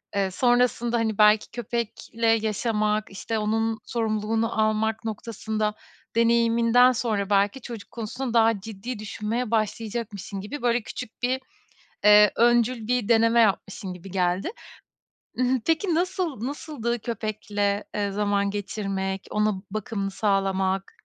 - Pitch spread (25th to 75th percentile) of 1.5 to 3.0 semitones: Yes, narrow, 2.5 semitones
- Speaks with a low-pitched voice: No, high, 220 Hz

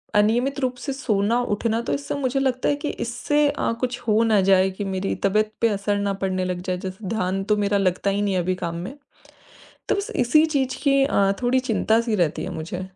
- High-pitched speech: Yes, high, 215 Hz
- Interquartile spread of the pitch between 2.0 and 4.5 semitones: No, average, 4.9 semitones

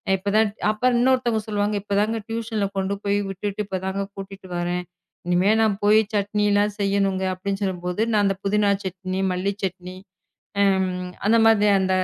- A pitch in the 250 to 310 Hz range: No, high, 200 Hz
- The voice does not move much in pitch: Yes, narrow, 1.9 semitones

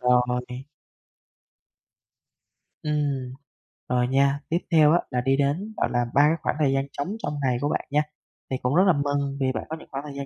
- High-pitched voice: No, medium, 140 Hz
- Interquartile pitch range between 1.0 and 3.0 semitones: Yes, narrow, 2.6 semitones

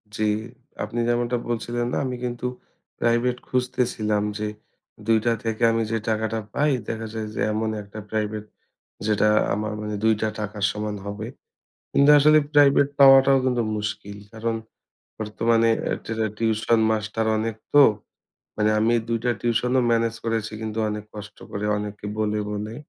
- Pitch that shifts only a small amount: Yes, narrow, 1.9 semitones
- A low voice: Yes, low, 110 Hz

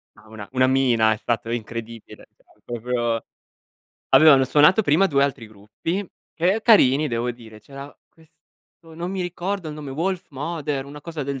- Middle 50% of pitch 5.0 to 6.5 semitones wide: Yes, wide, 5.6 semitones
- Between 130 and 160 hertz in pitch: Yes, medium, 140 Hz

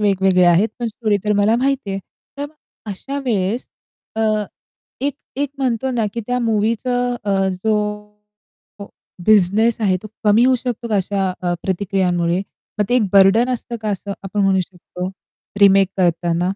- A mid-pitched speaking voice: No, high, 205 Hz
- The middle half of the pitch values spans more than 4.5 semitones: No, average, 3.7 semitones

